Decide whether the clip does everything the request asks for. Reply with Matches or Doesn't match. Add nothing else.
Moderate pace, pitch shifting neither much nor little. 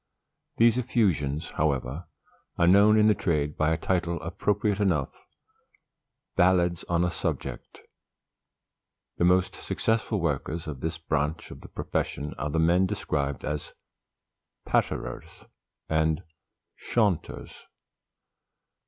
Doesn't match